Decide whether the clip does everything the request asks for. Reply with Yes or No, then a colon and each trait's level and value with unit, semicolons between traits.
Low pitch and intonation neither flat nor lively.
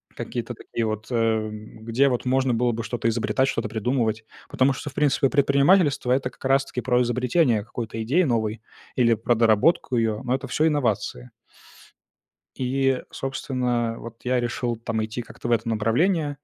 Yes: low, 120 Hz; average, 3.0 semitones